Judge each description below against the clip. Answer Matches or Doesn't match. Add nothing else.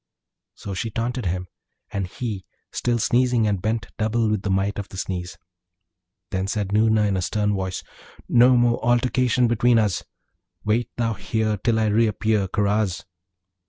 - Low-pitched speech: Matches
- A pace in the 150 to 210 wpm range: Matches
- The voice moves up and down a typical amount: Matches